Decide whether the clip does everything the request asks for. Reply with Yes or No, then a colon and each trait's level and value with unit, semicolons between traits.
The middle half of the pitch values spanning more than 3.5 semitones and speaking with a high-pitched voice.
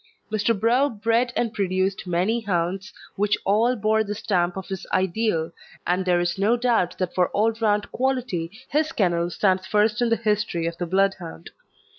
Yes: average, 3.9 semitones; high, 205 Hz